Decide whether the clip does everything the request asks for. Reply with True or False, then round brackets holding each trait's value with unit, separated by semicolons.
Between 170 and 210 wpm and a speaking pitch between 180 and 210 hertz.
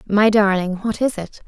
True (205 wpm; 205 Hz)